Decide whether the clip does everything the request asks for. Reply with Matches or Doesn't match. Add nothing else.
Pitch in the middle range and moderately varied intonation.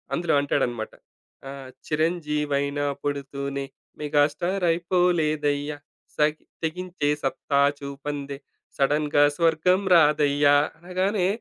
Matches